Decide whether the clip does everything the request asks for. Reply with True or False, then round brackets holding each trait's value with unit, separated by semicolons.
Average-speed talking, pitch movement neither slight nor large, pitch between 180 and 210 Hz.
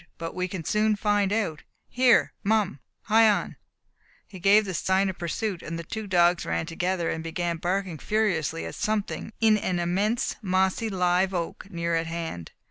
True (175 wpm; 3.7 semitones; 185 Hz)